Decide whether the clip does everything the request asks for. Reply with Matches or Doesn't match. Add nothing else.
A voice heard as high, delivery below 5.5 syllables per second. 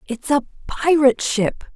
Matches